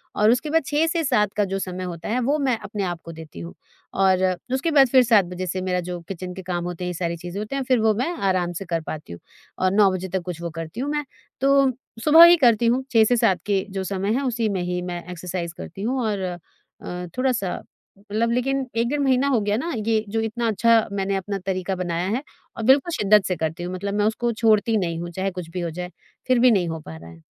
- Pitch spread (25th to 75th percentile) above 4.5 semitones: Yes, average, 5.0 semitones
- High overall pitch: Yes, high, 200 Hz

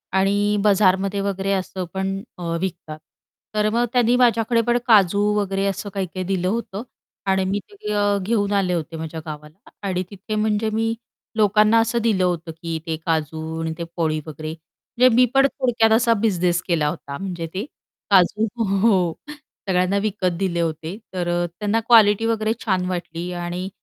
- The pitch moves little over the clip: No, average, 3.7 semitones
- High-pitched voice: Yes, high, 195 Hz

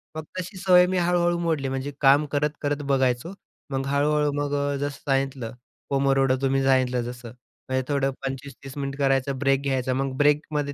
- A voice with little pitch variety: Yes, narrow, 1.6 semitones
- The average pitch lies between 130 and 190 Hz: Yes, medium, 140 Hz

